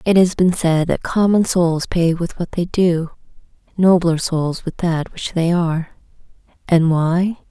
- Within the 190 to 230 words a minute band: No, average, 170 wpm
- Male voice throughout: No, female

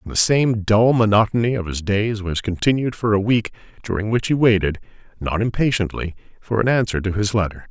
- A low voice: Yes, low, 105 Hz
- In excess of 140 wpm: Yes, average, 195 wpm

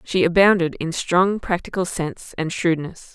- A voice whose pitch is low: No, medium, 175 Hz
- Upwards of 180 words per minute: No, average, 155 wpm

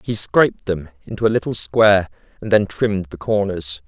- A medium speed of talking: Yes, average, 185 wpm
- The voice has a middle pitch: No, low, 100 Hz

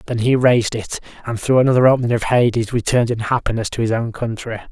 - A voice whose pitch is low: Yes, low, 115 Hz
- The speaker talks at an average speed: No, fast, 215 wpm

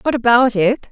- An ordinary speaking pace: Yes, average, 195 wpm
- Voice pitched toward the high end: Yes, high, 235 Hz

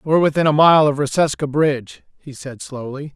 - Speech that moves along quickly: No, average, 190 wpm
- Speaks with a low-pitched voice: No, medium, 145 Hz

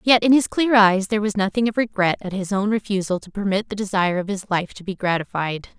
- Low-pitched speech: No, high, 200 Hz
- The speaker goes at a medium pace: No, fast, 250 wpm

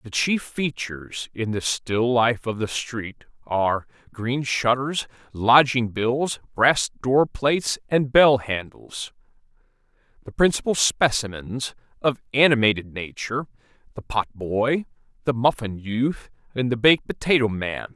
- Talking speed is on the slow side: Yes, slow, 125 wpm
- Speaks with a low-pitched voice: Yes, low, 120 Hz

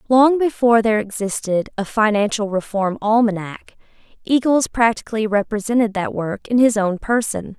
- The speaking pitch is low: No, high, 220 Hz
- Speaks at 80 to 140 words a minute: Yes, slow, 135 wpm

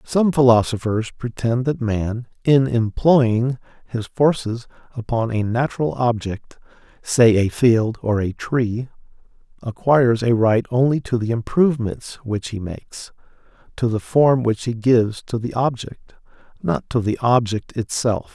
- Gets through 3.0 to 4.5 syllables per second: Yes, 4.3 syllables/s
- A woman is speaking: No, male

